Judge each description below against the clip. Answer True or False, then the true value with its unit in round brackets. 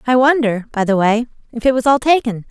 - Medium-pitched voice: False (240 Hz)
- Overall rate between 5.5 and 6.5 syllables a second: True (5.9 syllables/s)